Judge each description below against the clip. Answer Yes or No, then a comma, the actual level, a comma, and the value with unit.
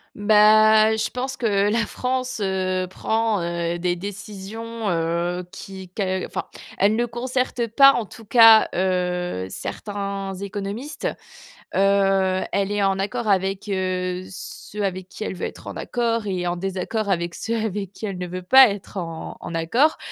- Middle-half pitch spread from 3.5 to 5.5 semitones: No, average, 3.0 semitones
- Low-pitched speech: No, high, 200 Hz